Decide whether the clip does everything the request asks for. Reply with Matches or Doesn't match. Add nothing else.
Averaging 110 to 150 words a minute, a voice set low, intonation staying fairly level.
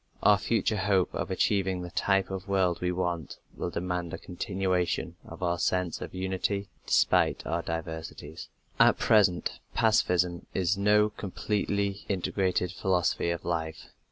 Matches